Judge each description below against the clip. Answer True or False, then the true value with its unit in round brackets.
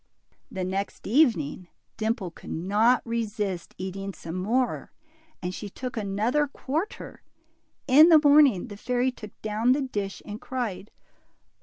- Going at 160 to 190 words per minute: False (135 wpm)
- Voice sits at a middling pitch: False (220 Hz)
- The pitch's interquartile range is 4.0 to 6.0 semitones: True (4.7 semitones)